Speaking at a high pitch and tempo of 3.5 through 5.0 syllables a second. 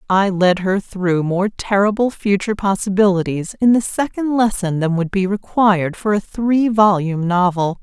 Yes: high, 195 Hz; 4.7 syllables/s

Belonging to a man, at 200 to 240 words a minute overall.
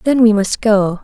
No: female; fast, 230 wpm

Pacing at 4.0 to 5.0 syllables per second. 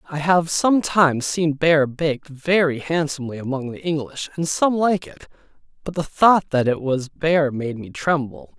Yes: 4.7 syllables/s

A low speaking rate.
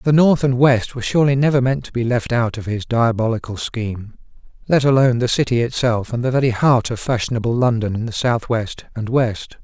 No: average, 200 wpm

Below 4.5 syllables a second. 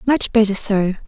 No: 4.6 syllables/s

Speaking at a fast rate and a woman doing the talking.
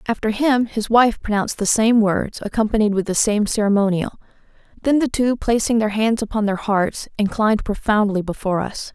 No: average, 175 wpm; female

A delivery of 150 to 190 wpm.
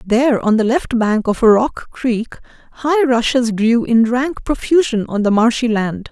Yes: average, 175 wpm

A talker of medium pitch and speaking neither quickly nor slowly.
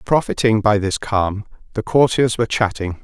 No: low, 110 Hz; average, 160 wpm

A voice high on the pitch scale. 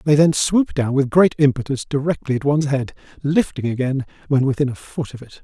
No: medium, 140 Hz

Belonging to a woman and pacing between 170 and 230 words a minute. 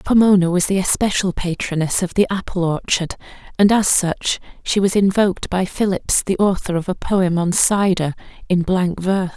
Yes: female; average, 175 wpm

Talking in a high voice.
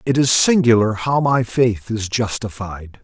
No: low, 115 Hz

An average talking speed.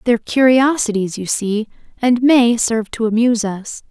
Yes: average, 155 wpm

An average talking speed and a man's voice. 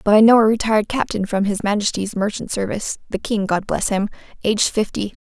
No: average, 185 wpm; female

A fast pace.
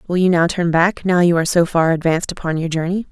Yes: fast, 270 wpm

